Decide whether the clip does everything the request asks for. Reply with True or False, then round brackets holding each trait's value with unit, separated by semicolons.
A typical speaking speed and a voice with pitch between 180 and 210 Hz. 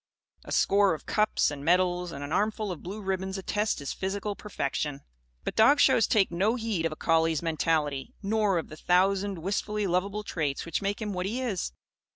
True (190 wpm; 190 Hz)